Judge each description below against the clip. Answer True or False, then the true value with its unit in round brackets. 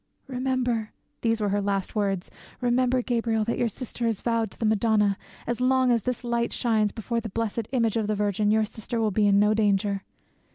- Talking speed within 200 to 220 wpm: True (205 wpm)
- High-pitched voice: True (225 Hz)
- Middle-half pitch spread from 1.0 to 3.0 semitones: True (2.4 semitones)